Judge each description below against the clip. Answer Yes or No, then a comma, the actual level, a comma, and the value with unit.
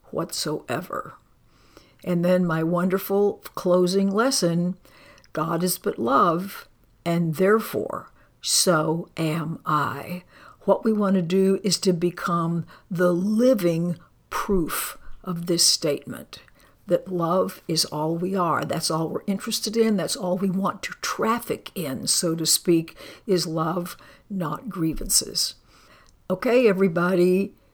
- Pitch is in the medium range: Yes, medium, 180 Hz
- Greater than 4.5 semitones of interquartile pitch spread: No, narrow, 2.6 semitones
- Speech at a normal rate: No, slow, 125 wpm